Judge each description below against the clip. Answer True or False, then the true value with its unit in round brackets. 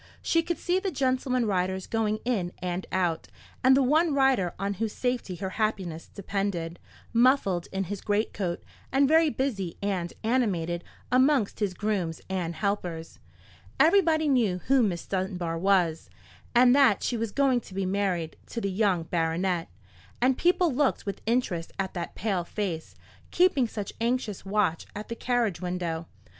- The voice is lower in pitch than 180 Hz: False (205 Hz)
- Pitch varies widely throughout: True (5.9 semitones)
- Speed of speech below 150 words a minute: False (155 wpm)